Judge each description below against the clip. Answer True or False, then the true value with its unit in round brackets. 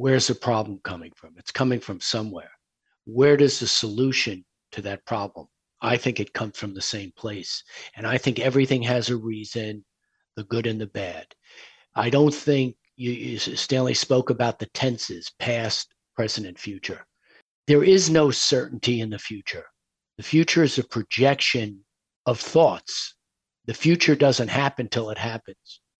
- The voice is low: True (120 Hz)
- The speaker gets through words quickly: False (165 wpm)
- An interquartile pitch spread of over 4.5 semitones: False (3.3 semitones)